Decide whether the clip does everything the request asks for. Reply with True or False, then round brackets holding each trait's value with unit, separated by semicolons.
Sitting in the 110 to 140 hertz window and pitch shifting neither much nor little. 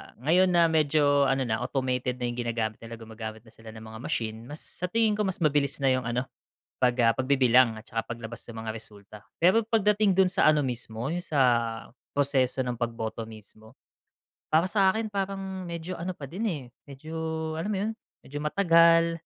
False (135 Hz; 6.8 semitones)